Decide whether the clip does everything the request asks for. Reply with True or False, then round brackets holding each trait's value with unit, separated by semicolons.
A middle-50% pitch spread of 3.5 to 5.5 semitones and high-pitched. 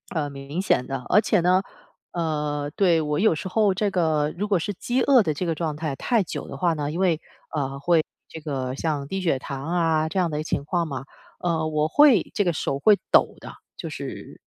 False (3.8 semitones; 160 Hz)